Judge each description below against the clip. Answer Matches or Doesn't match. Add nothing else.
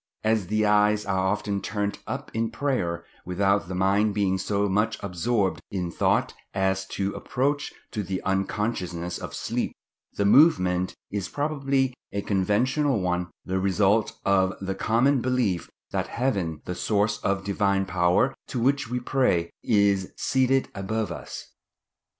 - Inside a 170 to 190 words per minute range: Doesn't match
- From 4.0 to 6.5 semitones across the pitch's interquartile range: Doesn't match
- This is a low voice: Matches